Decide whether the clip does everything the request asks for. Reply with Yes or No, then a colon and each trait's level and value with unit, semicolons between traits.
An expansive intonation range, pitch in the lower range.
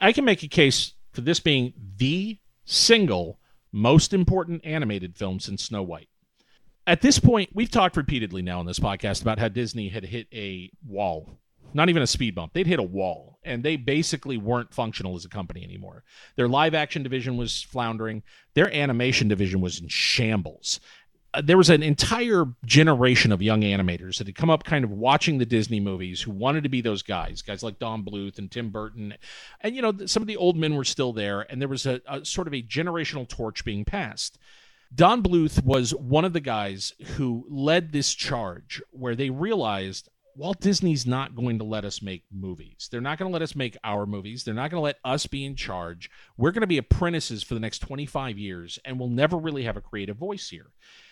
Yes: wide, 6.7 semitones; low, 125 Hz